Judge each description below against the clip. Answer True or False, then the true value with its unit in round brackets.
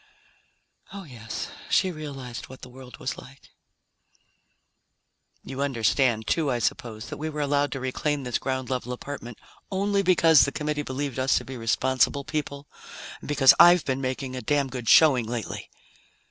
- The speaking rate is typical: True (160 wpm)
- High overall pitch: False (135 Hz)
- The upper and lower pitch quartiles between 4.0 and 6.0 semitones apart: False (2.7 semitones)